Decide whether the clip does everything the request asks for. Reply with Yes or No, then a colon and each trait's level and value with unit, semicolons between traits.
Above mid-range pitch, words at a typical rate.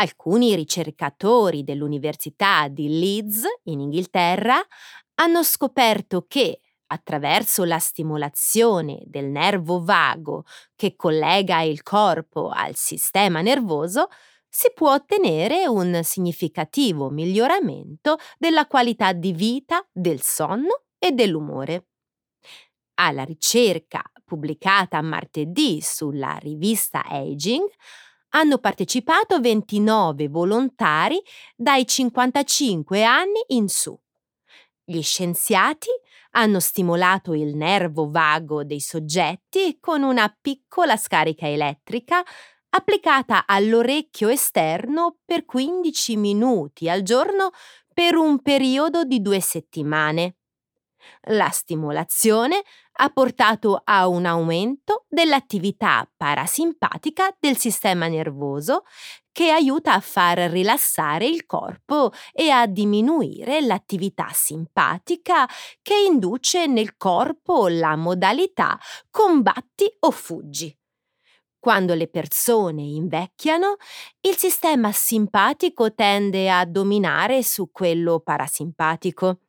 No: high, 210 Hz; slow, 95 wpm